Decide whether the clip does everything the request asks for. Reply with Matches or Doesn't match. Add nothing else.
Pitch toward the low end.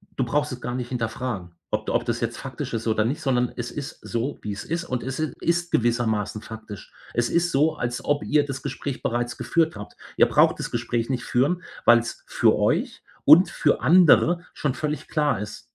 Matches